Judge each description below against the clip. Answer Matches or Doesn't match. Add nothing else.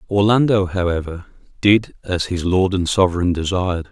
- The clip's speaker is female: Doesn't match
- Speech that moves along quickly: Doesn't match